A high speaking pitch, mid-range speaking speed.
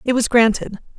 Yes: high, 230 Hz; average, 185 wpm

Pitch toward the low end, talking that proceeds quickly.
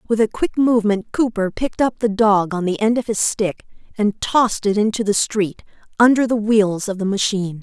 No: high, 210 Hz; fast, 215 wpm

